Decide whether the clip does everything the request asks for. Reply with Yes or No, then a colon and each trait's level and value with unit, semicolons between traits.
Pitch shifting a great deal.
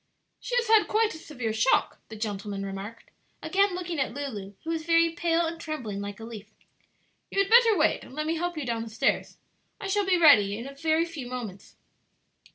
Yes: wide, 7.5 semitones